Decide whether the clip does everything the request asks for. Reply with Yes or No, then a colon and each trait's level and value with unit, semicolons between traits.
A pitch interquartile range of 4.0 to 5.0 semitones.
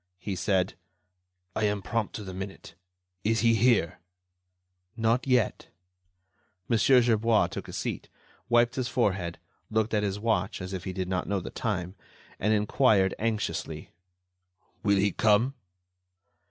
No: average, 3.2 semitones